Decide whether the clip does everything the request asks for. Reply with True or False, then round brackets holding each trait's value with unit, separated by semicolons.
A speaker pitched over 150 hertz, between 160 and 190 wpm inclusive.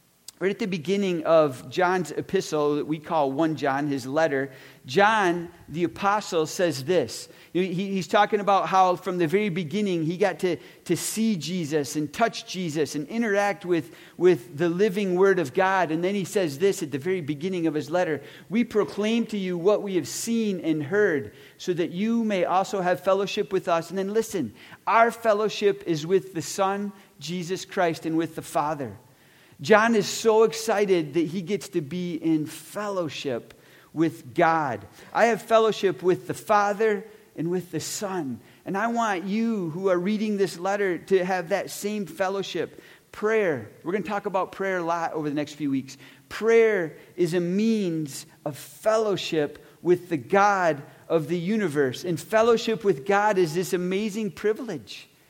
True (185 Hz; 175 wpm)